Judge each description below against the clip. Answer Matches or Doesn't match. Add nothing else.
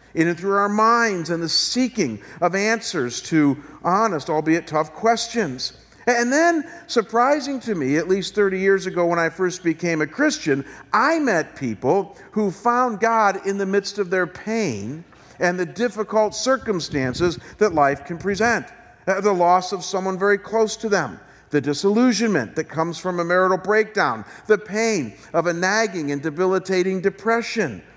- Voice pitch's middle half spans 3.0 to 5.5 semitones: Matches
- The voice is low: Doesn't match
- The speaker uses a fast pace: Doesn't match